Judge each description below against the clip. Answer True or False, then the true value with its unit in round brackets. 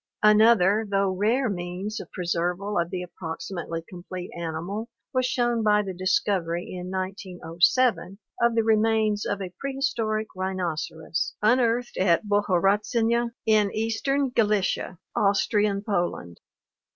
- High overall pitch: True (200 Hz)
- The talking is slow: True (115 wpm)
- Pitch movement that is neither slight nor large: True (3.8 semitones)